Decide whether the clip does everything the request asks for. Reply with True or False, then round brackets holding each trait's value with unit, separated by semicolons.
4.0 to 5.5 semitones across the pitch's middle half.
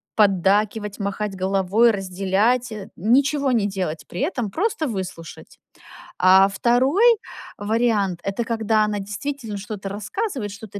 False (3.5 semitones)